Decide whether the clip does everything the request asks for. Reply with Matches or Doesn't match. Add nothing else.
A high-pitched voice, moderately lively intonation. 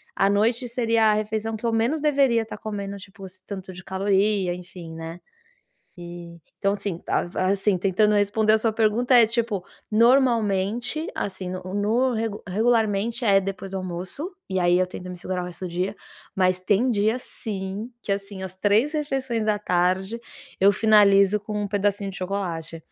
Matches